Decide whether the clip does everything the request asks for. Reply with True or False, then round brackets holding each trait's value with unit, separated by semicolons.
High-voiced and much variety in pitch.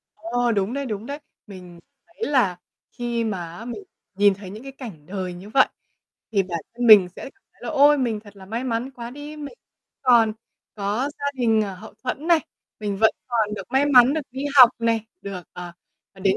False (225 Hz; 4.7 semitones)